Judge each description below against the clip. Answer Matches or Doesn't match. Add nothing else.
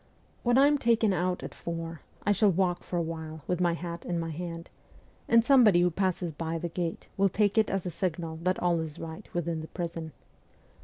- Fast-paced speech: Matches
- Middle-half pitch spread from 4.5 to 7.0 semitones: Doesn't match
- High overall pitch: Doesn't match